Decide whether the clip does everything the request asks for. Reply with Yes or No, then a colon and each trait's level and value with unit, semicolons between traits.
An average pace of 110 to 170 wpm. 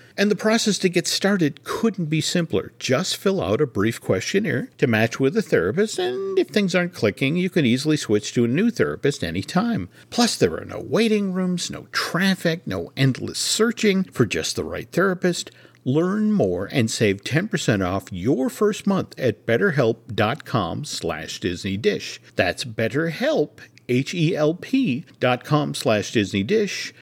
Yes: average, 150 wpm